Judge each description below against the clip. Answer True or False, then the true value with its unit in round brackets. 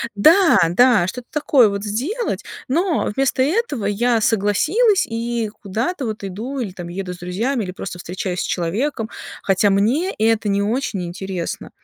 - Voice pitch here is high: True (220 Hz)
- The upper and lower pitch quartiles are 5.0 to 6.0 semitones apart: True (5.5 semitones)